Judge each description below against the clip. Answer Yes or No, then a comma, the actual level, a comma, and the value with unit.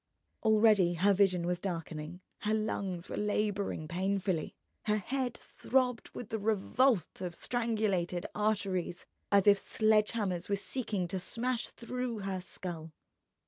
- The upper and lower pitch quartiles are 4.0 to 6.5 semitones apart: No, average, 3.4 semitones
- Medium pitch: No, high, 200 Hz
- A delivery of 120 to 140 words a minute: Yes, slow, 135 wpm